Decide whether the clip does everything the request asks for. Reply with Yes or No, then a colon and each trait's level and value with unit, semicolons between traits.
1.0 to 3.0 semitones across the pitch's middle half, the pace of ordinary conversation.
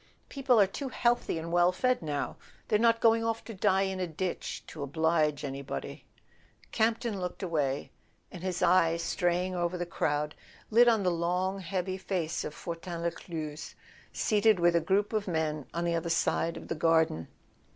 No: average, 3.5 semitones; average, 175 wpm